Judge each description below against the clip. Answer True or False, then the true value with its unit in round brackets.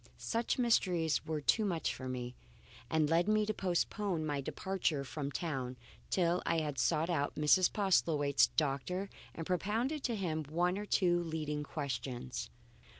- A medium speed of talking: True (150 wpm)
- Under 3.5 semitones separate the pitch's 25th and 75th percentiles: False (4.4 semitones)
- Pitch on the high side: False (165 Hz)